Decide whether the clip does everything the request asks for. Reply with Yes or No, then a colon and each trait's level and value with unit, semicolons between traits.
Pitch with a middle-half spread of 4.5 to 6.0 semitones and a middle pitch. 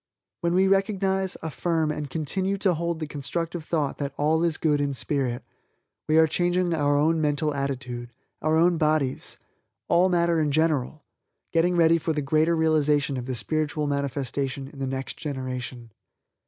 No: average, 3.2 semitones; medium, 155 Hz